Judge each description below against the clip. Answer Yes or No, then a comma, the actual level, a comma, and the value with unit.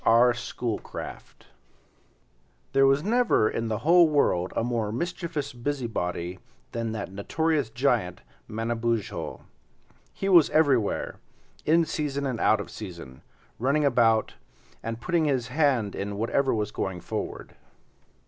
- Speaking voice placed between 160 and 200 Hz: No, low, 120 Hz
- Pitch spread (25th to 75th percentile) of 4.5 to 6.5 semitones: Yes, average, 5.1 semitones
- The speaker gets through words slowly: Yes, slow, 125 wpm